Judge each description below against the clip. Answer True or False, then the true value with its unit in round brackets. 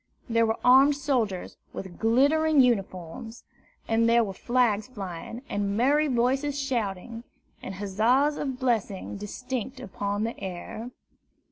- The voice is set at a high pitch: True (230 Hz)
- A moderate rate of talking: False (125 wpm)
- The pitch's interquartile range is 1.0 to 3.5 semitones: False (4.4 semitones)